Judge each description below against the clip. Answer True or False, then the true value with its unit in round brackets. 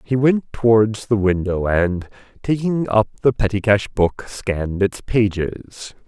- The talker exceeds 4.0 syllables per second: False (3.9 syllables/s)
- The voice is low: True (105 Hz)